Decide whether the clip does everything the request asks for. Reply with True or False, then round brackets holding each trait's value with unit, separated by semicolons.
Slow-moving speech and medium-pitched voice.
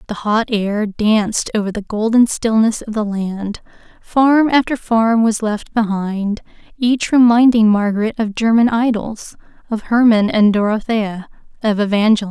False (130 wpm; 220 Hz)